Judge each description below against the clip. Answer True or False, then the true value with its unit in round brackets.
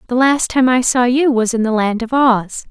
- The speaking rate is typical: False (265 wpm)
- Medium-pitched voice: False (245 Hz)